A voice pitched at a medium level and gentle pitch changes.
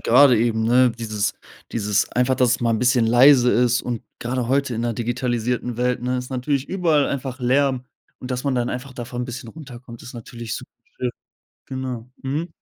No: low, 125 Hz; narrow, 1.7 semitones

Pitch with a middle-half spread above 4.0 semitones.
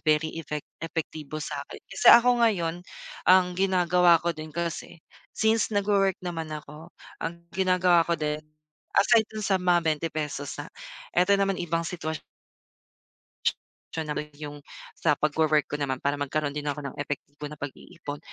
No: average, 3.3 semitones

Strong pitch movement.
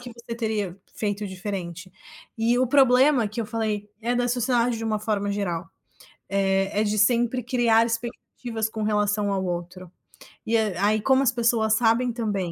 No: average, 2.9 semitones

